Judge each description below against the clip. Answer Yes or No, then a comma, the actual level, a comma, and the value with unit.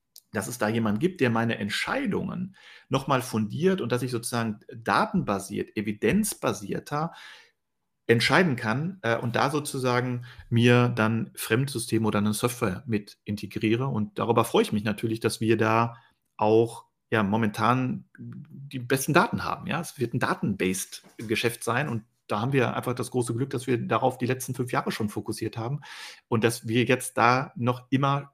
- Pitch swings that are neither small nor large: Yes, average, 3.3 semitones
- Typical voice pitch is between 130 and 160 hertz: No, low, 120 Hz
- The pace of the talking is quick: No, average, 165 wpm